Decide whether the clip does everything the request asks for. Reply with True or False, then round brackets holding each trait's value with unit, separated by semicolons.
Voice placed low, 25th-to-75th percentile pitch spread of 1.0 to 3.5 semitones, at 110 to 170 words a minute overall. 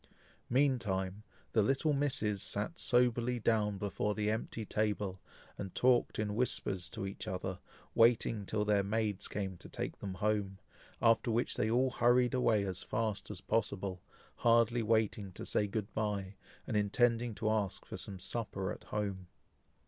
True (105 Hz; 2.9 semitones; 155 wpm)